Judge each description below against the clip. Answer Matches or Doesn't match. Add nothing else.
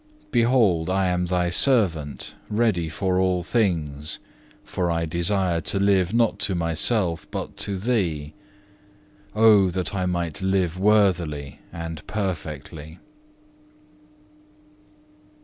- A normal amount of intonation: Matches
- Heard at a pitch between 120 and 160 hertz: Doesn't match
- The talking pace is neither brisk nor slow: Doesn't match